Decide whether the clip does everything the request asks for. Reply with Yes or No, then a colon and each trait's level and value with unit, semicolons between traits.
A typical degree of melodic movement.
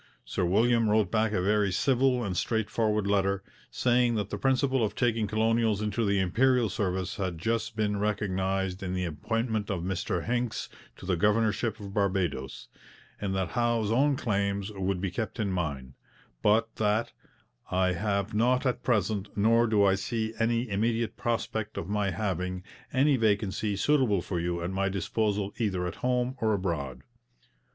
Yes: average, 3.2 semitones